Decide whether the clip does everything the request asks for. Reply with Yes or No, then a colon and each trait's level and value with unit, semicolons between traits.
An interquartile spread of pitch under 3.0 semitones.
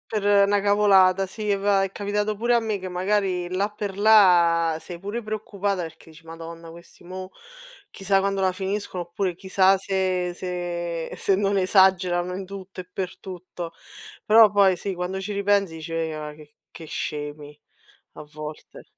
Yes: narrow, 2.6 semitones